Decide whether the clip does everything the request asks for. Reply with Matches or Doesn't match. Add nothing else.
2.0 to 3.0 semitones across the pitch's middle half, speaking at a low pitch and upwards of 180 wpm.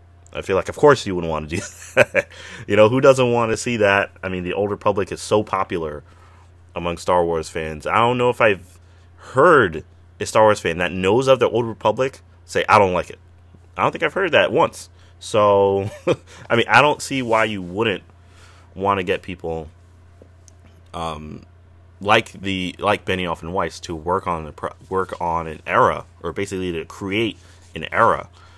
Matches